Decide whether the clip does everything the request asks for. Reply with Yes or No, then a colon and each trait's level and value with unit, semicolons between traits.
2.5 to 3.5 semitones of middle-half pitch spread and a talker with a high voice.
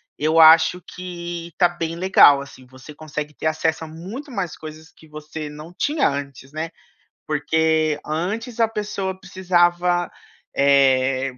No: average, 2.9 semitones; medium, 160 Hz